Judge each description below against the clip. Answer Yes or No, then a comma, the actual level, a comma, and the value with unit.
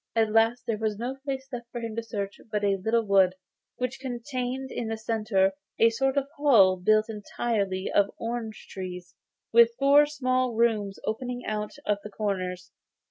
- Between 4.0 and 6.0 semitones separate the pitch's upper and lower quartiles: No, average, 3.3 semitones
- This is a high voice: Yes, high, 225 Hz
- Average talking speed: Yes, average, 175 wpm